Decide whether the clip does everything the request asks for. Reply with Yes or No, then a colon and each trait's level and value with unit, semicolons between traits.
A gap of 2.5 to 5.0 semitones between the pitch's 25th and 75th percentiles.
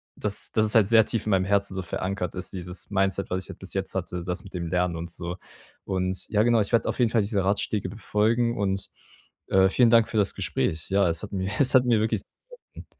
Yes: average, 2.9 semitones